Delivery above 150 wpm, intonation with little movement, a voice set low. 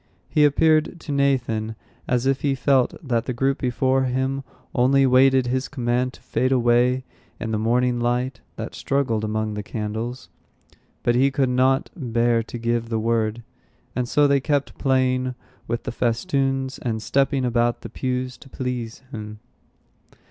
Yes: average, 160 wpm; narrow, 2.3 semitones; low, 125 Hz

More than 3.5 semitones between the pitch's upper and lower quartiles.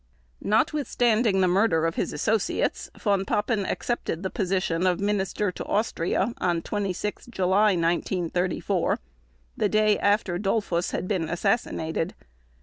No: average, 3.1 semitones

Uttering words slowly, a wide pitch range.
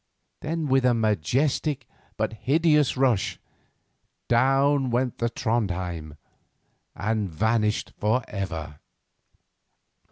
No: slow, 90 wpm; average, 4.9 semitones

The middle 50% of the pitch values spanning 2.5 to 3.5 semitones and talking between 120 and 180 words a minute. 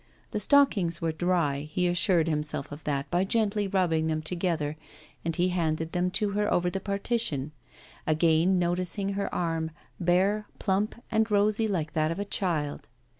No: average, 3.9 semitones; average, 165 wpm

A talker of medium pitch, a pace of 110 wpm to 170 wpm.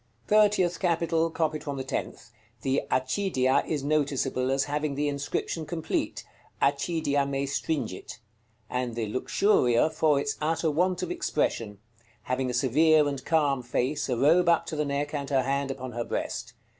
Yes: medium, 145 Hz; average, 160 wpm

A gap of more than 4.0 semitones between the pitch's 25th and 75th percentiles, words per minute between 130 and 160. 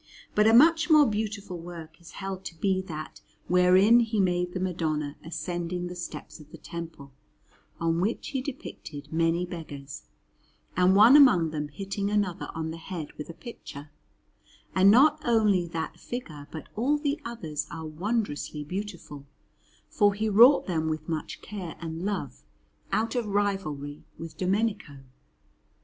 Yes: average, 4.8 semitones; average, 155 wpm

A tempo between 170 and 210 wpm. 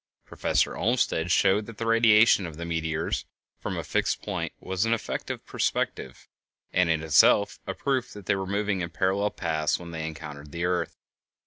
Yes: average, 185 wpm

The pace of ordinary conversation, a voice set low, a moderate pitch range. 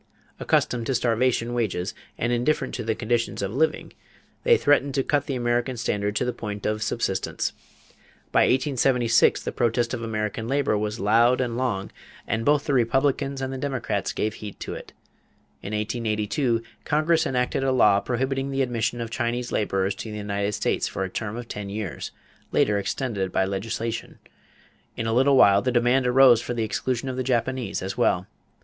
Yes: average, 180 wpm; low, 120 Hz; average, 3.4 semitones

